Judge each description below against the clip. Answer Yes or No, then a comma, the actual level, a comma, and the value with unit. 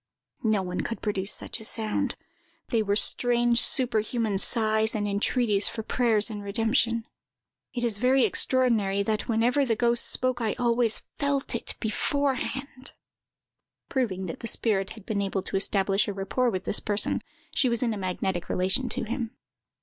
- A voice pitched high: Yes, high, 225 Hz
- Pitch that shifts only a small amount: No, average, 3.2 semitones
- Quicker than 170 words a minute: No, average, 165 wpm